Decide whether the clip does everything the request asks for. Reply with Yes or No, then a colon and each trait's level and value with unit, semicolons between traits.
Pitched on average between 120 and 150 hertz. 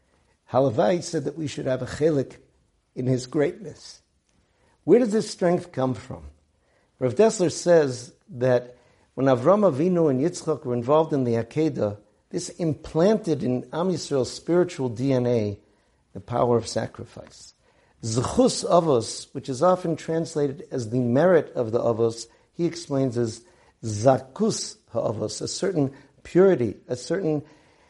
Yes: low, 135 Hz